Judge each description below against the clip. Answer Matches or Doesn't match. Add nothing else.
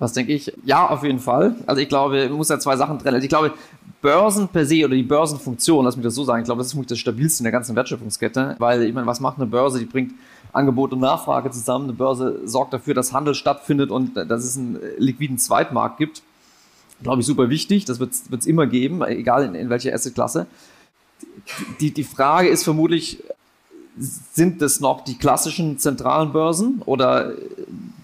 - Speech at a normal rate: Doesn't match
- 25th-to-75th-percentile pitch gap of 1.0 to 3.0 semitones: Doesn't match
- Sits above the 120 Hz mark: Matches